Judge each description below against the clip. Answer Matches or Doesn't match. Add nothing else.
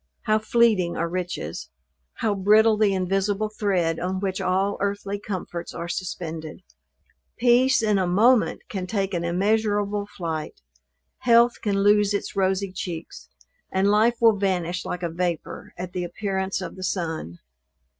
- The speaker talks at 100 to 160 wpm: Matches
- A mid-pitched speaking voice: Doesn't match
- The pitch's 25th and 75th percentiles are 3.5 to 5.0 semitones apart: Doesn't match